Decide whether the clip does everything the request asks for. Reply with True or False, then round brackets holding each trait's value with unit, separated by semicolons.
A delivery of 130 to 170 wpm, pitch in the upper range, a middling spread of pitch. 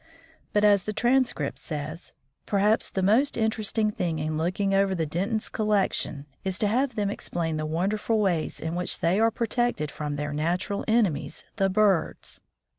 True (165 wpm; 195 Hz; 4.8 semitones)